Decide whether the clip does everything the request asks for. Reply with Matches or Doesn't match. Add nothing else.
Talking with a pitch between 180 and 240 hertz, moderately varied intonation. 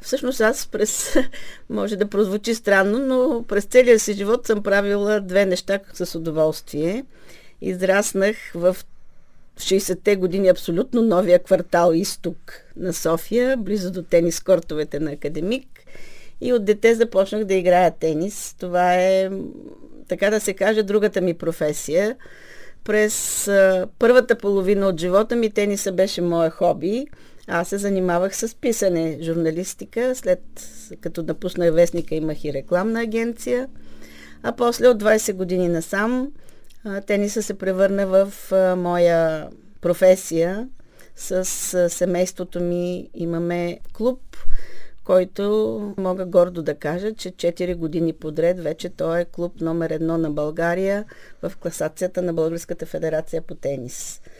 Matches